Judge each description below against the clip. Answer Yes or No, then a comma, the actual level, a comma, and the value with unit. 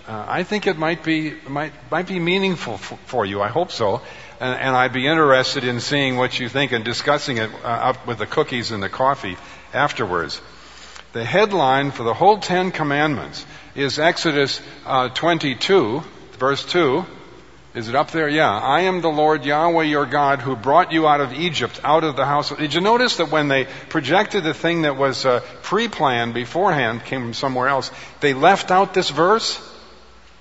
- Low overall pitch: No, medium, 145 Hz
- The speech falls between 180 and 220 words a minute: Yes, average, 195 wpm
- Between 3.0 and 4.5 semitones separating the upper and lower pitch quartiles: Yes, average, 4.2 semitones